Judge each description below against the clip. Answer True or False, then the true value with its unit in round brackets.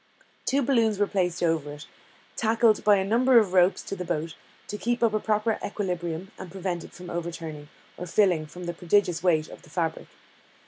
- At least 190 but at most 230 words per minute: True (195 wpm)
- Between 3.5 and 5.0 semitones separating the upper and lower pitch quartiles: True (4.1 semitones)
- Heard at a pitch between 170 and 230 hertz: True (185 Hz)